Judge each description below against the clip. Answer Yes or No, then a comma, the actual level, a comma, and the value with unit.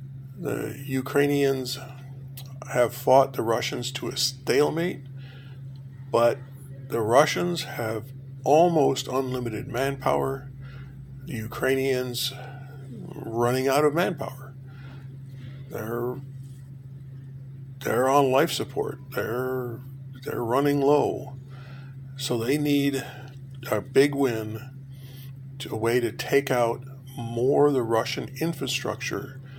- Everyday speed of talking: No, slow, 95 wpm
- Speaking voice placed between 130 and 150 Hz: Yes, low, 135 Hz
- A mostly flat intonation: Yes, narrow, 0.7 semitones